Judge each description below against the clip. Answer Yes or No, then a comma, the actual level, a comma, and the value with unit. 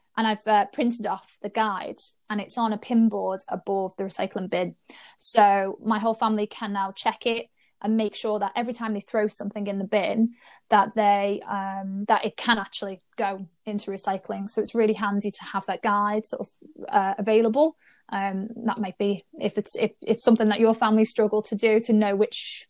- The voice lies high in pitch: Yes, high, 210 Hz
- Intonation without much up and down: Yes, narrow, 2.0 semitones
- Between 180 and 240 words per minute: Yes, fast, 205 wpm